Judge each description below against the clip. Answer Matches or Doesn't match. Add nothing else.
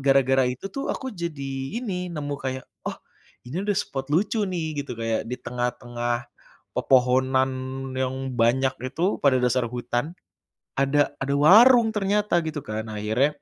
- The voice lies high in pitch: Doesn't match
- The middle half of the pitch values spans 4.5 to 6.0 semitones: Matches